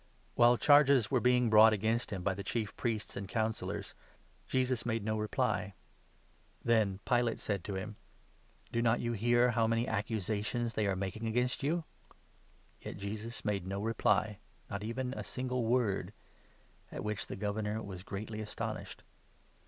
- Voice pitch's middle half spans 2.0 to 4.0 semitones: Yes, narrow, 2.6 semitones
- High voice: No, low, 110 Hz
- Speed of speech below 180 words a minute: Yes, average, 165 wpm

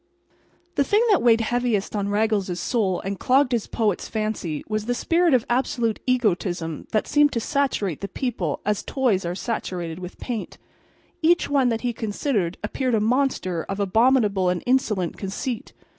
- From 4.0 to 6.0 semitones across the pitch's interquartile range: Yes, average, 4.7 semitones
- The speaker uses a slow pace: No, average, 165 wpm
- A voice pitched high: Yes, high, 220 Hz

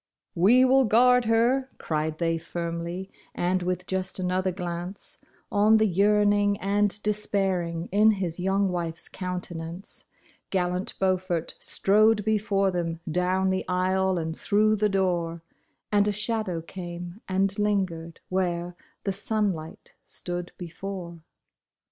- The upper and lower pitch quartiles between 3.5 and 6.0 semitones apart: No, average, 2.9 semitones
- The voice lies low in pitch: No, medium, 185 Hz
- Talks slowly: Yes, slow, 125 wpm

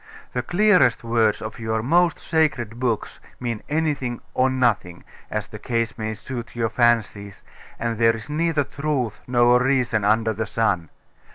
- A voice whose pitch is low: Yes, low, 120 Hz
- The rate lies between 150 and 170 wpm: Yes, average, 155 wpm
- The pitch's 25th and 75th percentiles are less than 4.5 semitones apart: Yes, average, 3.0 semitones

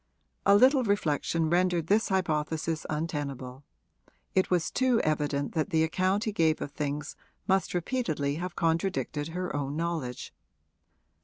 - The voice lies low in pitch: No, medium, 165 Hz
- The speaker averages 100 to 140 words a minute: Yes, slow, 135 wpm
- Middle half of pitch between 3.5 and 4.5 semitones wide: Yes, average, 4.0 semitones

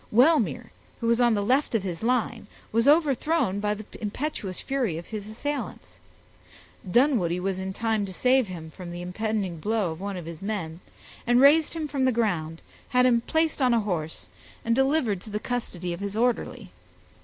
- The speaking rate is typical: Yes, average, 190 wpm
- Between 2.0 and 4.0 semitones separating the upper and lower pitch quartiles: No, average, 5.2 semitones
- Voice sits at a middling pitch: No, high, 220 Hz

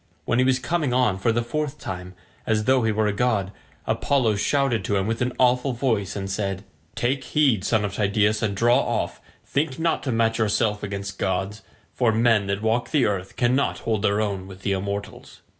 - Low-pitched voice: Yes, low, 110 Hz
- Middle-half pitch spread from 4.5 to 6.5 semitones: No, average, 3.8 semitones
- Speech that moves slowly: No, fast, 205 wpm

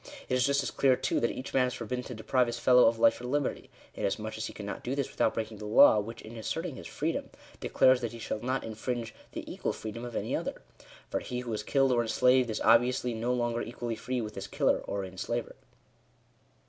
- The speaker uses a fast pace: Yes, fast, 235 wpm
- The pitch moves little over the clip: Yes, narrow, 2.1 semitones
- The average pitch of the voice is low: Yes, low, 120 Hz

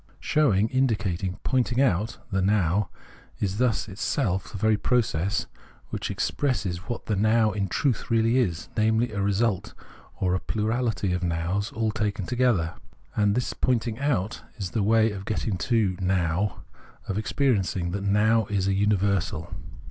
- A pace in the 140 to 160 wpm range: Yes, average, 155 wpm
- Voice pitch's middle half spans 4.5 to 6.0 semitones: No, average, 3.1 semitones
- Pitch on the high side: No, low, 105 Hz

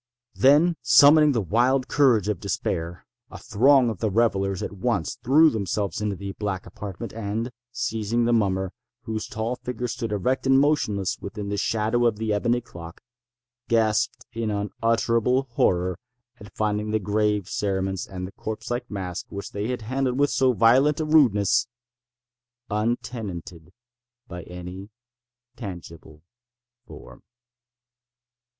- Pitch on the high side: No, low, 110 Hz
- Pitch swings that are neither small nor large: Yes, average, 3.8 semitones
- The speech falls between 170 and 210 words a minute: No, slow, 135 wpm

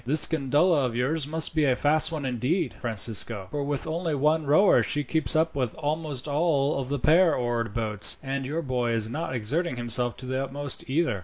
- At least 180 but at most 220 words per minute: Yes, average, 200 wpm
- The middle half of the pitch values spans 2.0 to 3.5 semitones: No, average, 4.2 semitones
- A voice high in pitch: No, medium, 140 Hz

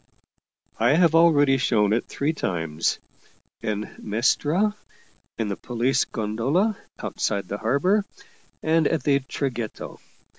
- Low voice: Yes, low, 130 Hz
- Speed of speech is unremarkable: No, slow, 120 wpm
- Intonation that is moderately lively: No, wide, 6.5 semitones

